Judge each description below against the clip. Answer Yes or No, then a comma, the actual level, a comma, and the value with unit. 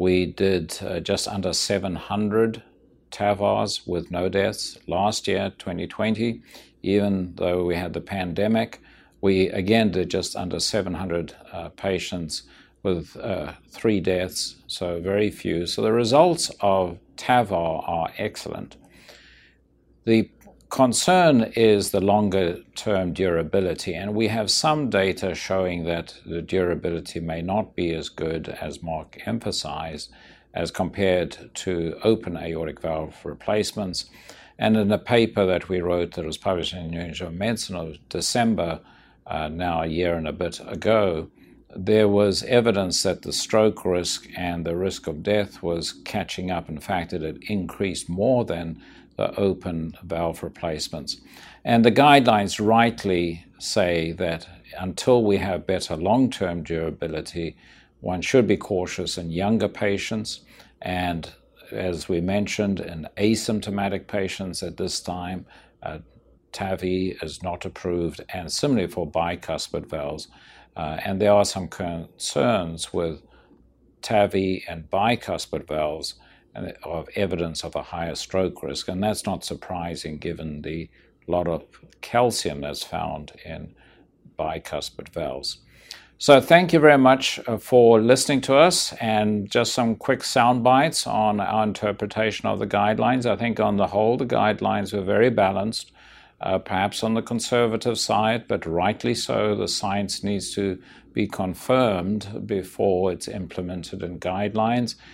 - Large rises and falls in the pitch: No, average, 3.9 semitones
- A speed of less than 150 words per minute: Yes, average, 140 wpm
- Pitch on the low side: Yes, very low, 95 Hz